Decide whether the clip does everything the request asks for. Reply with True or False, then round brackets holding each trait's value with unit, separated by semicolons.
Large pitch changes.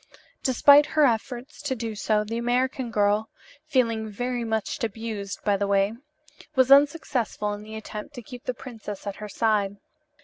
False (3.3 semitones)